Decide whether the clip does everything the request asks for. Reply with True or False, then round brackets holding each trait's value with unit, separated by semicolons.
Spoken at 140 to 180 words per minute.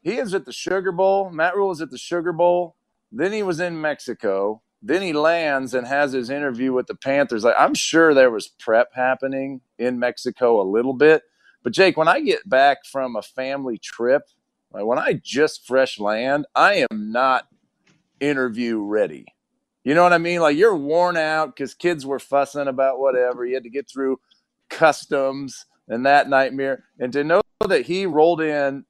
False (190 wpm)